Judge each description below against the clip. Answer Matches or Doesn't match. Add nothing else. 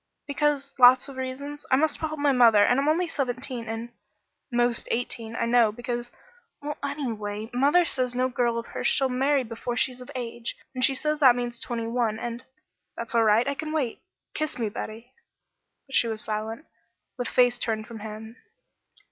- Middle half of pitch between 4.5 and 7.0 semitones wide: Doesn't match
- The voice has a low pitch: Doesn't match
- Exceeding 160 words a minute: Matches